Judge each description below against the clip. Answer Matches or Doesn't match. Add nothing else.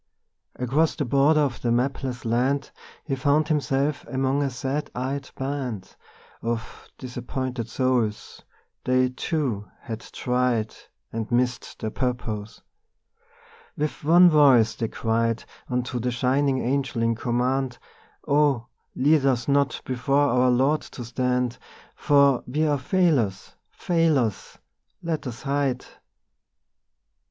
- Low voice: Matches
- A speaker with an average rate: Doesn't match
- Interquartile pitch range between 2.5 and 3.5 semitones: Matches